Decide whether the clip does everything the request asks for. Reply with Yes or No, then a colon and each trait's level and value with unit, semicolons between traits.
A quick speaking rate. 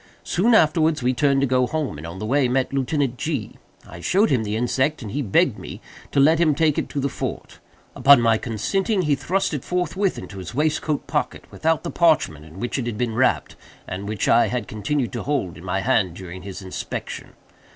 Yes: fast, 215 wpm